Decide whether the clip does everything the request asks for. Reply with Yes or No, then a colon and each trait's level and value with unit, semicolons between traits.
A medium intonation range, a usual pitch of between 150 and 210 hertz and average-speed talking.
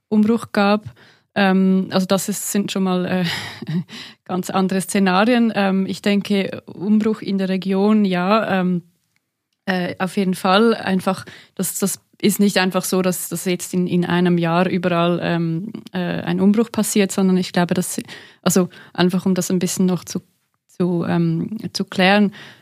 No: narrow, 2.0 semitones; high, 190 Hz; average, 165 wpm